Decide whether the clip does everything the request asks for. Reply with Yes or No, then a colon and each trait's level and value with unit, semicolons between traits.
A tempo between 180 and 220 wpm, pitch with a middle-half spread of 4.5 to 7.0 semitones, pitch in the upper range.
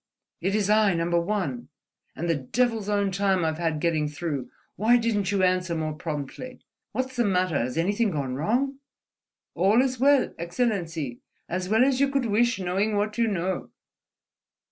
No: average, 165 wpm; wide, 5.4 semitones; high, 195 Hz